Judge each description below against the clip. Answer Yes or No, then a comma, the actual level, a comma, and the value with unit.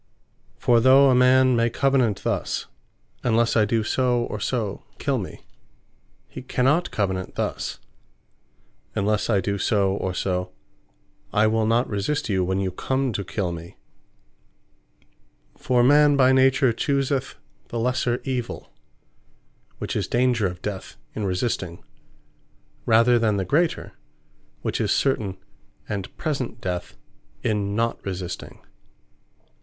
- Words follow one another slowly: Yes, slow, 130 wpm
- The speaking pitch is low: Yes, low, 115 Hz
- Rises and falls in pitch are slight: No, average, 4.6 semitones